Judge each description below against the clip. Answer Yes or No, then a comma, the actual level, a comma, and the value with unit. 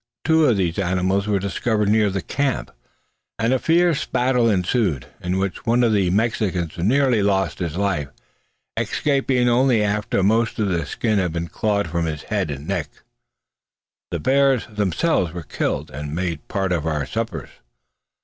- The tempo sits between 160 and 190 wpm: Yes, average, 165 wpm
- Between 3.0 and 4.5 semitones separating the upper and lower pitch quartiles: No, average, 5.1 semitones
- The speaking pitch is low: Yes, low, 100 Hz